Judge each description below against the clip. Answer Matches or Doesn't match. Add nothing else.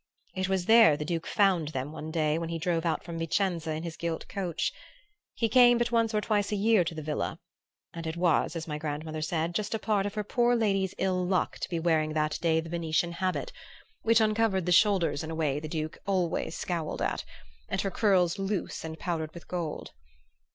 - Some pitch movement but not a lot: Matches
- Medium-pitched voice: Matches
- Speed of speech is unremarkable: Doesn't match